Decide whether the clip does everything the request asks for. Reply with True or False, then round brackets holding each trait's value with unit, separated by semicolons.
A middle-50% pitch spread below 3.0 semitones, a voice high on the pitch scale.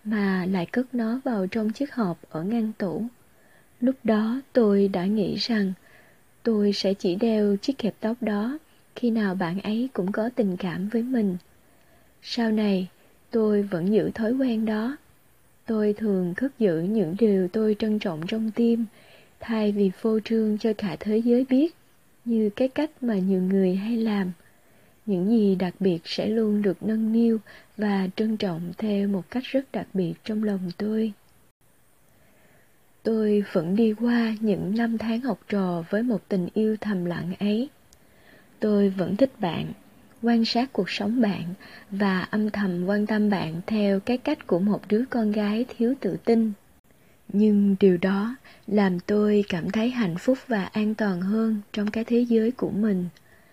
True (2.6 semitones; 215 Hz)